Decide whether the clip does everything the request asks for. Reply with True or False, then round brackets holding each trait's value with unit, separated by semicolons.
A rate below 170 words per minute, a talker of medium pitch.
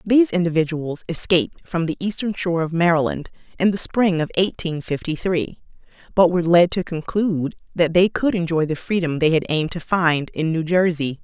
False (185 wpm; 170 Hz)